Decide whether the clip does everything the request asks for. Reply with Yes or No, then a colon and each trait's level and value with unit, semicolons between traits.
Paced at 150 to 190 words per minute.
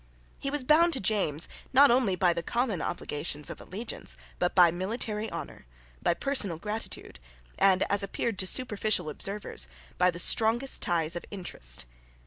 Yes: average, 155 wpm